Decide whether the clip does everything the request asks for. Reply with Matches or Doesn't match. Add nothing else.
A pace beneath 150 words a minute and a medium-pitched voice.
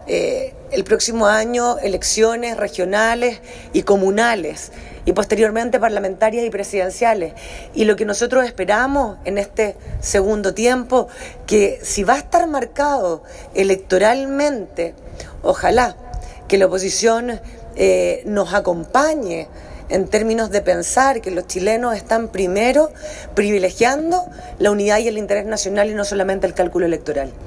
Doesn't match